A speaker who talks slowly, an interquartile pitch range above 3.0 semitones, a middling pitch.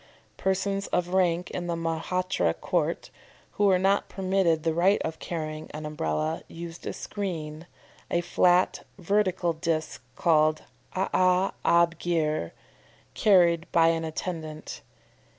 No: slow, 125 wpm; narrow, 2.5 semitones; medium, 170 Hz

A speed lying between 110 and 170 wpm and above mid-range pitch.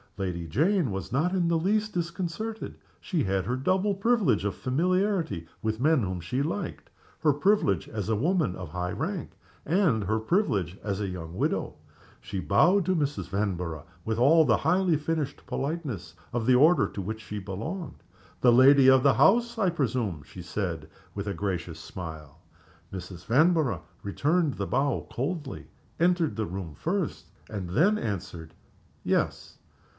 No: average, 160 wpm; low, 125 Hz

